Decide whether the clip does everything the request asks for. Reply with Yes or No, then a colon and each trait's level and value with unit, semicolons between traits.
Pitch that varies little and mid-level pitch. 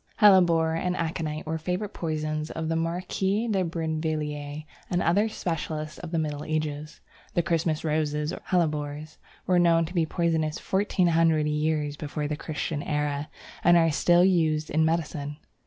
Yes: narrow, 2.1 semitones; medium, 160 Hz